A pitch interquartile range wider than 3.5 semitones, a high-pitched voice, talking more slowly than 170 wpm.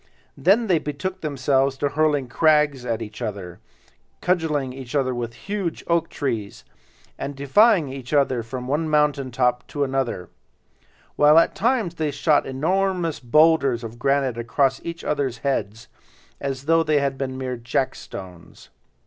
No: average, 4.0 semitones; medium, 140 Hz; average, 145 wpm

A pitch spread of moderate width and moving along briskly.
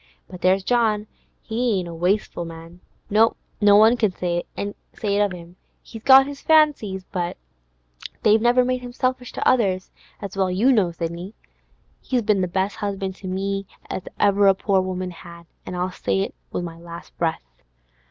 No: average, 3.7 semitones; average, 175 wpm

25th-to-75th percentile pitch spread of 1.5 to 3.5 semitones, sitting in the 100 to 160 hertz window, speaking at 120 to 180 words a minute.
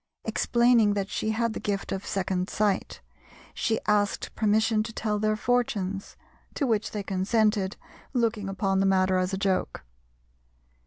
No: narrow, 2.4 semitones; high, 210 Hz; average, 150 wpm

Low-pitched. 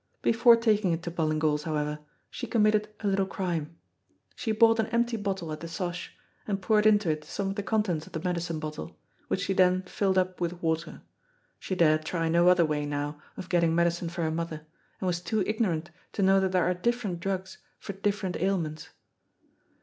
No: medium, 180 Hz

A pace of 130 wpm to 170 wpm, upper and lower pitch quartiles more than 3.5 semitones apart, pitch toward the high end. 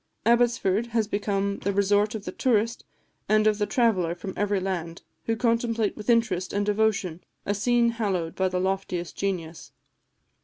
No: average, 160 wpm; average, 3.2 semitones; high, 205 Hz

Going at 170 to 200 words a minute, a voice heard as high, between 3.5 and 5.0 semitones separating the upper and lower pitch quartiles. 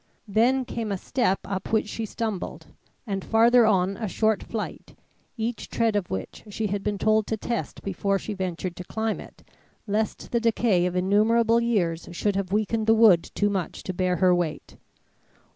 No: average, 180 wpm; high, 210 Hz; average, 3.1 semitones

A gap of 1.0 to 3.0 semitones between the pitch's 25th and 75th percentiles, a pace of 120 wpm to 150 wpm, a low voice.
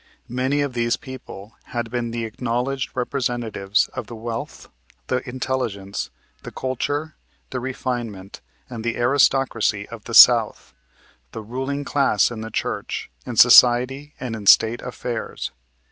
Yes: narrow, 2.6 semitones; slow, 135 wpm; low, 120 Hz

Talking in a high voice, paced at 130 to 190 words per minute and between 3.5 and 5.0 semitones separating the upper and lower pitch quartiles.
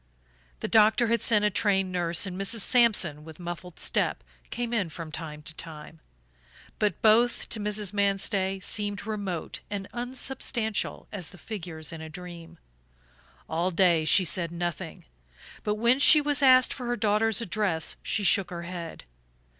Yes: high, 195 Hz; average, 160 wpm; average, 4.4 semitones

